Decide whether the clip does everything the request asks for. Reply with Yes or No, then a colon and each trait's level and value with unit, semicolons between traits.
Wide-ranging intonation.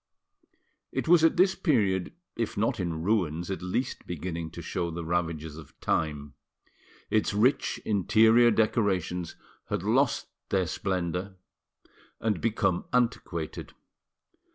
No: average, 4.7 semitones